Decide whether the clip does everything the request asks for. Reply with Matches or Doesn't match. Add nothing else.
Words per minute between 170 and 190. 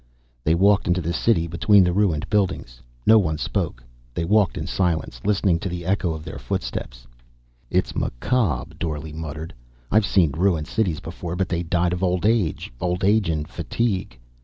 Matches